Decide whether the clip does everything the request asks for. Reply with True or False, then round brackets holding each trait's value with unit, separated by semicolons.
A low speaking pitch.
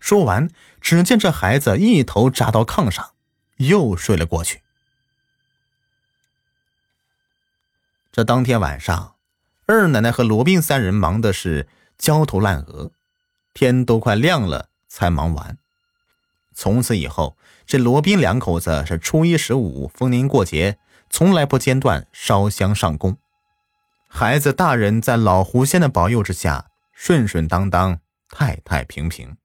True (125 Hz)